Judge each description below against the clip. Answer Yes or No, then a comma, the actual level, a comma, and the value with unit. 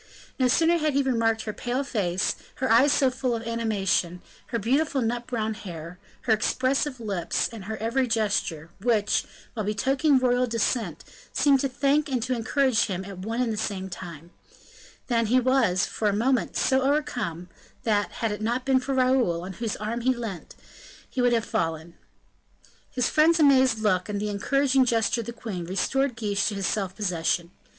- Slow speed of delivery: No, average, 185 wpm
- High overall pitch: Yes, high, 230 Hz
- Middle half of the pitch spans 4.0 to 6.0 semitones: Yes, average, 4.3 semitones